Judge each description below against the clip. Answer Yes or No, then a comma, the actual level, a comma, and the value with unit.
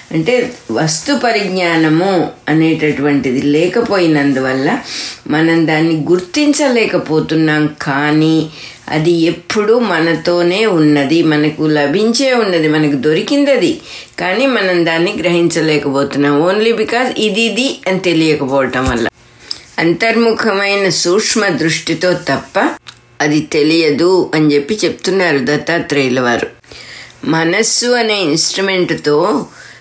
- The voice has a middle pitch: Yes, medium, 165 Hz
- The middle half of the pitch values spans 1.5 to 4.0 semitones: No, average, 4.7 semitones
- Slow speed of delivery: Yes, slow, 85 wpm